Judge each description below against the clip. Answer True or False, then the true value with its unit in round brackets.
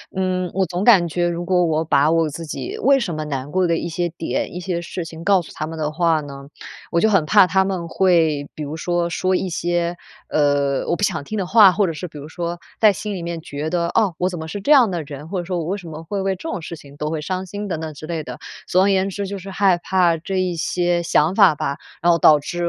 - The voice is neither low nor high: True (175 Hz)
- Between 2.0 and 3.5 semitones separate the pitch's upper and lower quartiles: True (3.0 semitones)